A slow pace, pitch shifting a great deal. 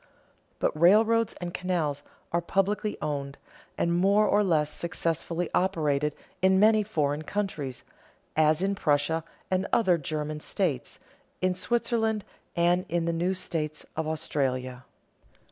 No: slow, 130 wpm; average, 4.2 semitones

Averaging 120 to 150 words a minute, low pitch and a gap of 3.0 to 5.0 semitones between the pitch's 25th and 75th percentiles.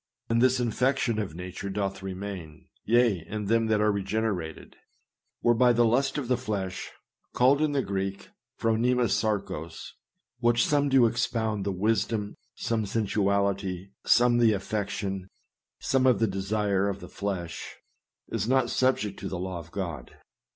Yes: average, 145 wpm; low, 105 Hz; average, 3.5 semitones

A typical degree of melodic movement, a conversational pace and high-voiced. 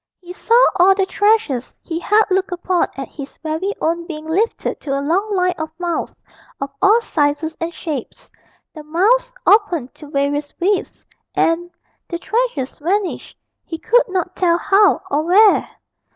Yes: average, 4.3 semitones; average, 160 wpm; very high, 345 Hz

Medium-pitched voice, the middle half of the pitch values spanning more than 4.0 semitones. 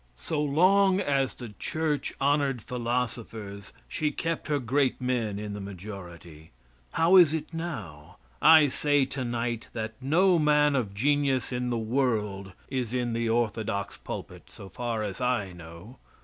No: low, 125 Hz; wide, 5.5 semitones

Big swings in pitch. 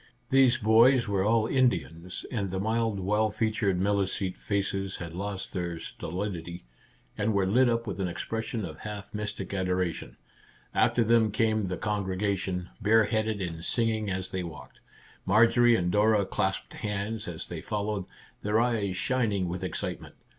No: average, 3.1 semitones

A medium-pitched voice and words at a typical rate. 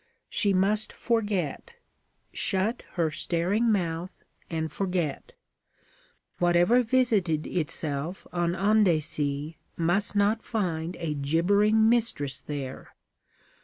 No: medium, 175 Hz; slow, 90 wpm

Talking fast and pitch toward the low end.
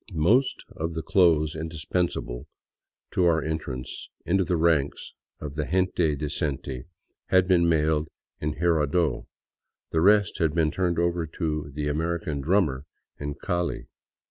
No: average, 140 wpm; very low, 80 Hz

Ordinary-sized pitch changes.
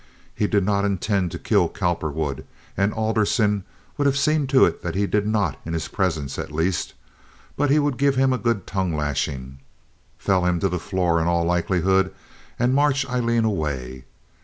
No: wide, 5.8 semitones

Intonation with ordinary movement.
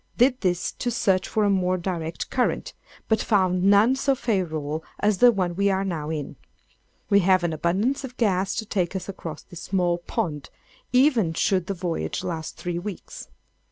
Yes: average, 3.5 semitones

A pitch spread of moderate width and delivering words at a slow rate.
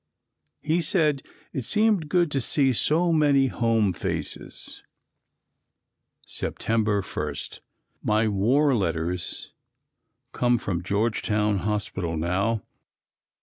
No: wide, 6.6 semitones; slow, 95 wpm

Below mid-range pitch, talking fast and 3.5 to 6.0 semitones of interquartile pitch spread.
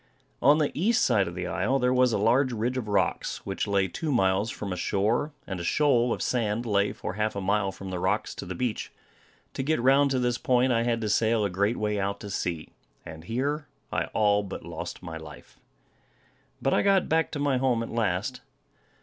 Yes: low, 110 Hz; fast, 220 wpm; average, 4.6 semitones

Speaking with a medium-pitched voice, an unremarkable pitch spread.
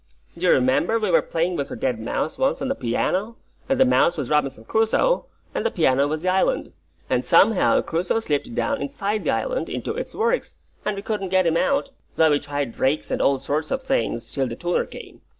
No: medium, 180 Hz; wide, 8.5 semitones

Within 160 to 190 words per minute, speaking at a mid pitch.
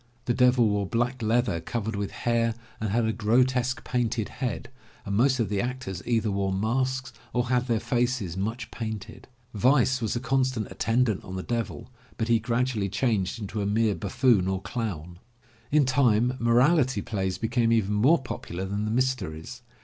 No: average, 175 wpm; low, 115 Hz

